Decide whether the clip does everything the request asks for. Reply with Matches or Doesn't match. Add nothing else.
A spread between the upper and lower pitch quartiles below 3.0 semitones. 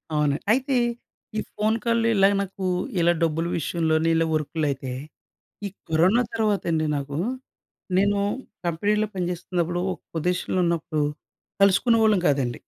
Doesn't match